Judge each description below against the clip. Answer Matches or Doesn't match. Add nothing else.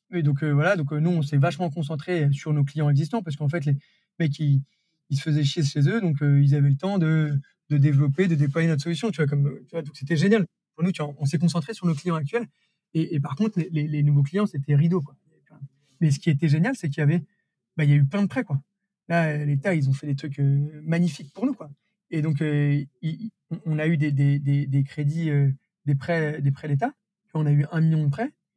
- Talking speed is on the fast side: Matches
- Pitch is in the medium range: Matches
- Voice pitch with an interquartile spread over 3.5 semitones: Doesn't match